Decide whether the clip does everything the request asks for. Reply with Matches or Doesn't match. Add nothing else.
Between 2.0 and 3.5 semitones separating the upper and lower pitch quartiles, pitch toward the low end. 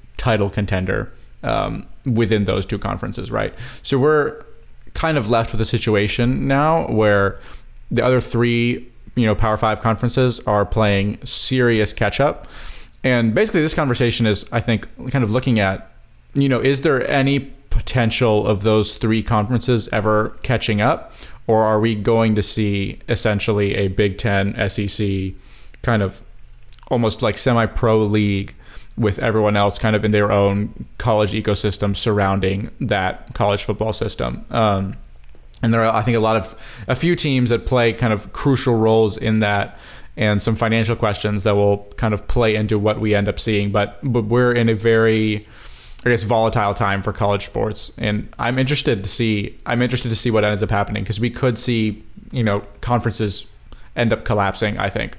Matches